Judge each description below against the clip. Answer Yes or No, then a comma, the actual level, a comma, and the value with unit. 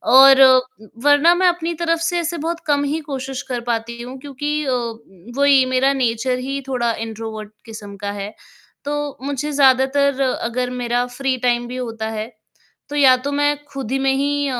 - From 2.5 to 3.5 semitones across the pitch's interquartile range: Yes, average, 3.1 semitones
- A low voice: No, very high, 265 Hz